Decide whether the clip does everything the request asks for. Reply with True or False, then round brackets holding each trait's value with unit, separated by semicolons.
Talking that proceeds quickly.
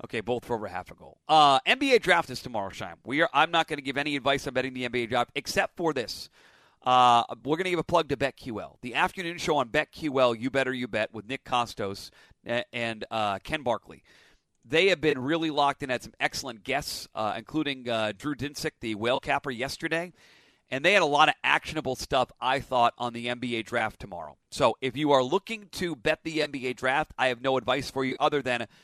True (225 wpm)